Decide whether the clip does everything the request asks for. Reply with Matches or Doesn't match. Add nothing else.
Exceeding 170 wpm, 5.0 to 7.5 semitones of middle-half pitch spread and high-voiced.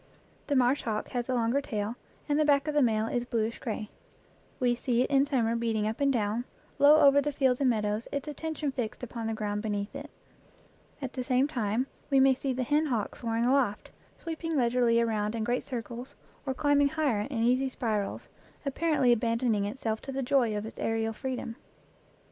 Doesn't match